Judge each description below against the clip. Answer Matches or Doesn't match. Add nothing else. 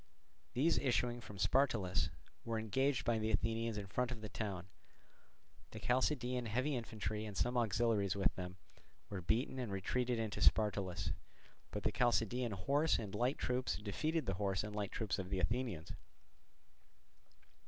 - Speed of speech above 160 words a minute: Doesn't match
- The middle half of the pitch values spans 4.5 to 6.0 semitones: Doesn't match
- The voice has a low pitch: Matches